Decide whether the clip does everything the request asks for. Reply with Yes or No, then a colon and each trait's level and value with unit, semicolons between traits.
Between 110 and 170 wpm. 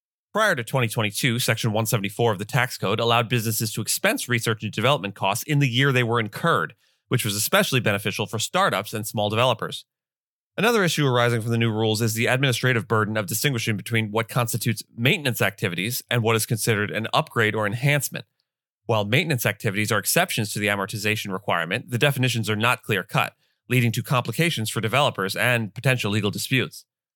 No: average, 180 wpm